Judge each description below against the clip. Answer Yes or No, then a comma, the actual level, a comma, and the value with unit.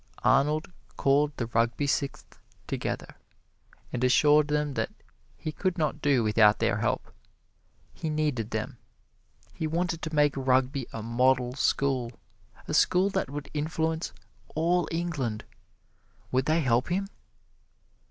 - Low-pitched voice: No, medium, 145 Hz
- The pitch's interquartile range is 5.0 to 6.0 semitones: No, average, 3.9 semitones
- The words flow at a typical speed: No, slow, 130 wpm